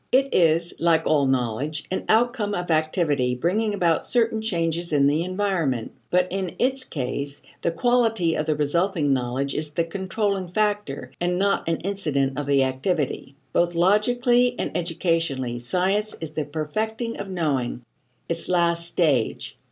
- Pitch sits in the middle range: Yes, medium, 170 Hz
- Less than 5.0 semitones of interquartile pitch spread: No, wide, 5.5 semitones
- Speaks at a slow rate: No, average, 150 wpm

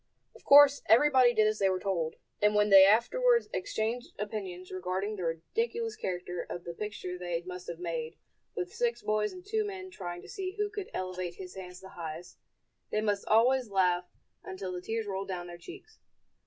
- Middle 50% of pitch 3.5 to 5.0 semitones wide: No, wide, 5.4 semitones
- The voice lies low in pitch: No, high, 200 Hz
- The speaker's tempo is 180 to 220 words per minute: Yes, average, 190 wpm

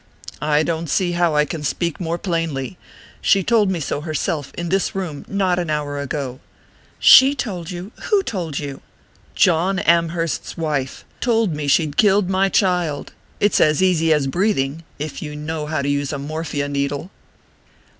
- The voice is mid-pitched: Yes, medium, 165 Hz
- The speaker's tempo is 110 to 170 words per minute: Yes, average, 165 wpm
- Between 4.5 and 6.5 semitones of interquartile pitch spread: No, average, 3.8 semitones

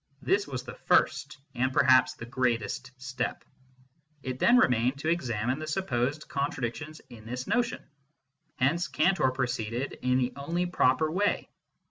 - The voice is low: Yes, low, 130 Hz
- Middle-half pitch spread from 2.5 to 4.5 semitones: Yes, average, 3.9 semitones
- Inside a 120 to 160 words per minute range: Yes, average, 140 wpm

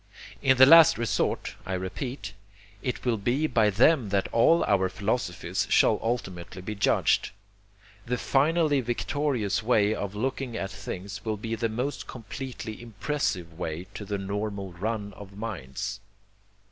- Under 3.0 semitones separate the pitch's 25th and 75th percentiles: No, average, 4.2 semitones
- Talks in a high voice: No, low, 110 Hz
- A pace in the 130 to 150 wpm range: Yes, average, 145 wpm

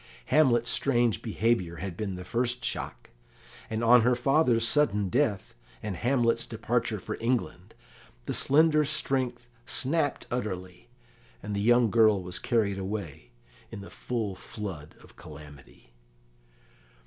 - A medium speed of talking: No, slow, 130 wpm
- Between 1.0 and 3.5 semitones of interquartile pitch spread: No, average, 4.1 semitones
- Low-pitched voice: Yes, low, 115 Hz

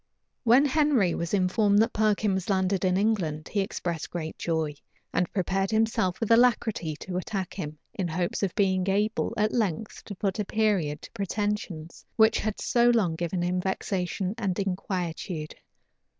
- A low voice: No, high, 195 Hz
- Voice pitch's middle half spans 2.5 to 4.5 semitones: Yes, average, 3.3 semitones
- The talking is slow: No, average, 165 wpm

